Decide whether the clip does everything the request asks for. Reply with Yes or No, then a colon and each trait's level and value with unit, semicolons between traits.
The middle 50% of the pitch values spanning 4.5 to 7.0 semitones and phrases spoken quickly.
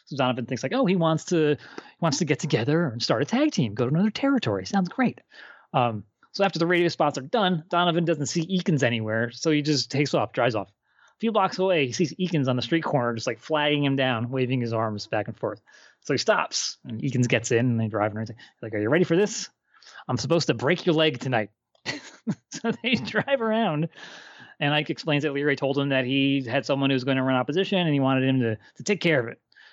Yes: average, 5.3 semitones; fast, 245 wpm